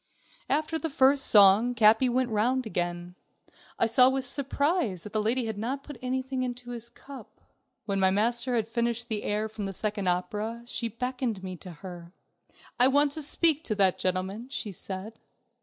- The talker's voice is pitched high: Yes, high, 230 Hz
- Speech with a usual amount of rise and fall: Yes, average, 4.1 semitones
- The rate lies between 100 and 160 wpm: No, average, 185 wpm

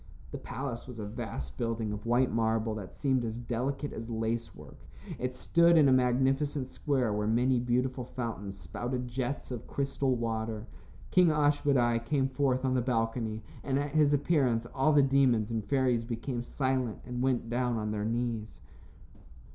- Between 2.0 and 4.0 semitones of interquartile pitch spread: Yes, average, 2.9 semitones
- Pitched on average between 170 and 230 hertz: No, low, 125 Hz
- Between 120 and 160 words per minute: No, average, 170 wpm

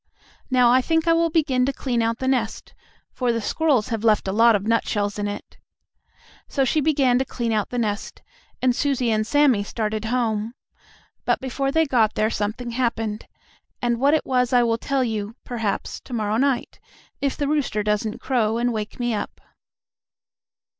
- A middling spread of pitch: Yes, average, 3.4 semitones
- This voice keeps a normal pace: Yes, average, 185 wpm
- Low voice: No, high, 240 Hz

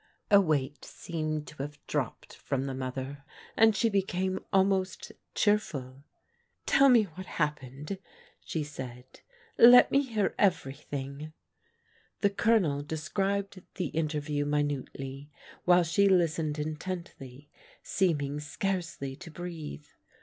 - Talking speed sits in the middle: No, slow, 120 wpm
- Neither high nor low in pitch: Yes, medium, 155 Hz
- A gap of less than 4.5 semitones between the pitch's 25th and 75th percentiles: No, average, 5.1 semitones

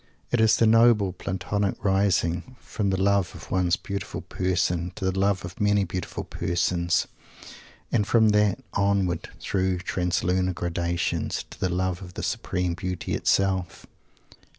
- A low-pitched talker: Yes, very low, 95 Hz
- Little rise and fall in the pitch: Yes, narrow, 2.2 semitones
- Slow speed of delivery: No, average, 145 wpm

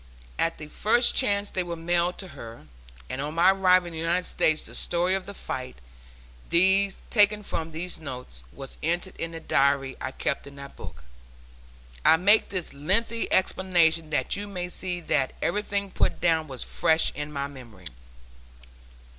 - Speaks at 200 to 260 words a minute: No, average, 170 wpm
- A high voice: No, medium, 170 Hz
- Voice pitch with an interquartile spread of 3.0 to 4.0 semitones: No, average, 4.9 semitones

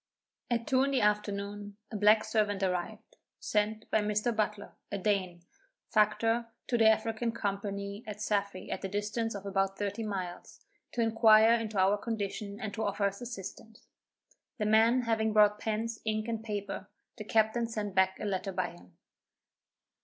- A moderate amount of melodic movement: No, narrow, 1.9 semitones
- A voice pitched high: Yes, high, 210 Hz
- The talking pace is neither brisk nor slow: Yes, average, 165 wpm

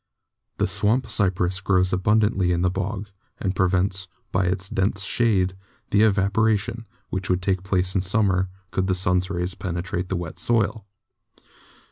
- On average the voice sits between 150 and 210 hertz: No, very low, 95 Hz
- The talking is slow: No, average, 155 wpm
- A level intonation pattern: Yes, narrow, 1.9 semitones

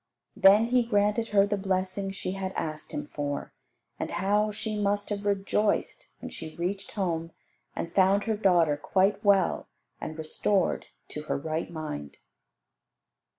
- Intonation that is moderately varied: Yes, average, 3.5 semitones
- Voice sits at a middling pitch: No, high, 195 Hz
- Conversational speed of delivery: Yes, average, 150 wpm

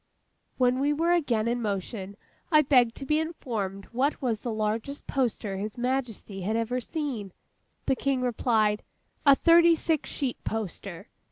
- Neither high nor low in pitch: No, high, 245 Hz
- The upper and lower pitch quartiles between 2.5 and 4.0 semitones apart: No, average, 4.6 semitones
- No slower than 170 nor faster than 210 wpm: No, average, 155 wpm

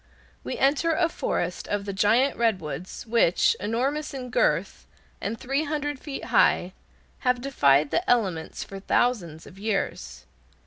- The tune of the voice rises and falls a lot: Yes, wide, 6.4 semitones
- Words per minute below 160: Yes, average, 140 wpm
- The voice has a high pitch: Yes, high, 230 Hz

